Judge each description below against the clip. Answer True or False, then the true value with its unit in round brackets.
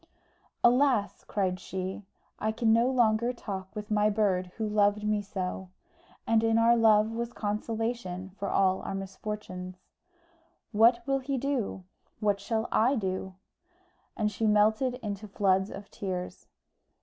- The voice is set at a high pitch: True (210 Hz)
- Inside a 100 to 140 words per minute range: True (135 wpm)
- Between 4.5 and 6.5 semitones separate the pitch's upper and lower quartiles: False (2.8 semitones)